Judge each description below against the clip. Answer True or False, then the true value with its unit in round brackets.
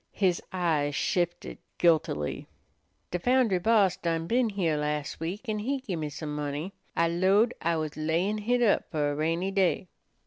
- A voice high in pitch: False (175 Hz)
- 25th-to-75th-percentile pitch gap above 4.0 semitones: True (4.7 semitones)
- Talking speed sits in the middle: True (165 wpm)